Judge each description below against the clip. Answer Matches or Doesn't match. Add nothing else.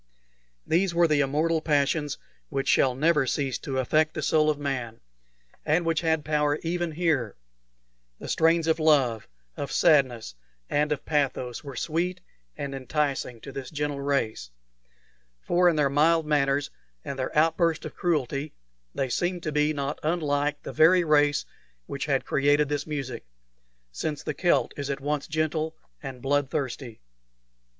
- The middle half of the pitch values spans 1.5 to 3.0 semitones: Matches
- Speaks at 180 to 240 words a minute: Doesn't match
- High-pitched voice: Doesn't match